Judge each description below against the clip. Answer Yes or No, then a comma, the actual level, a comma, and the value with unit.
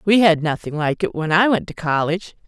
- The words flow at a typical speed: No, fast, 240 wpm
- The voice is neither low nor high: Yes, medium, 175 Hz